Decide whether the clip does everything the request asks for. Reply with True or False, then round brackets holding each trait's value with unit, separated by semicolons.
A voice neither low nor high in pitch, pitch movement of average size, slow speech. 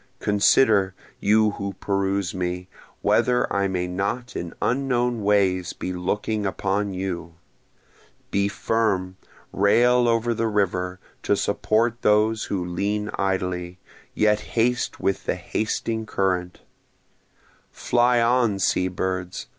False (100 Hz; 3.3 semitones; 115 wpm)